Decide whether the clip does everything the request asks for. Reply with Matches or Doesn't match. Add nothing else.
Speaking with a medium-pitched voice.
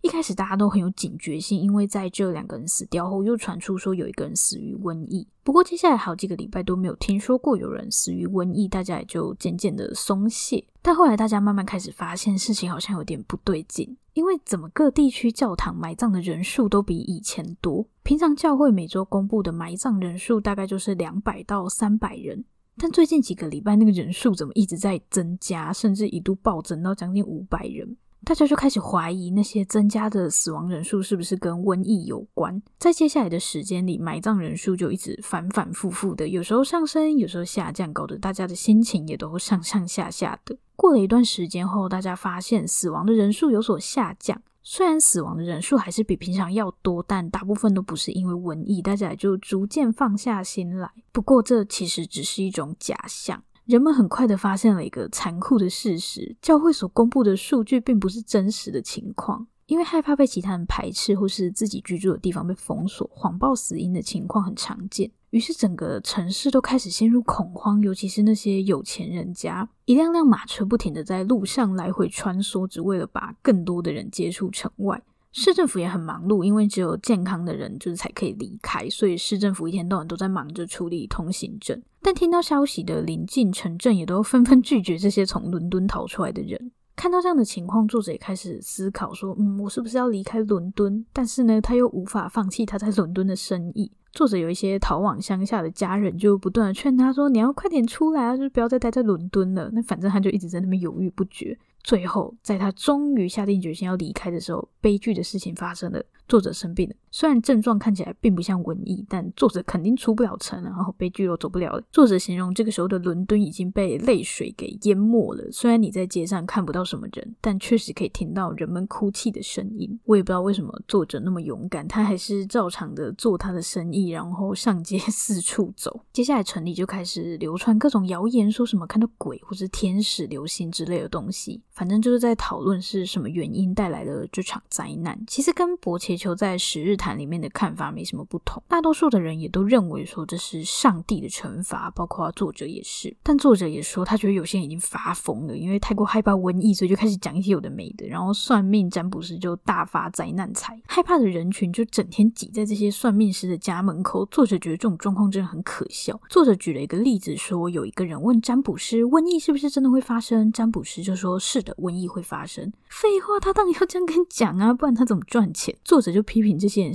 Doesn't match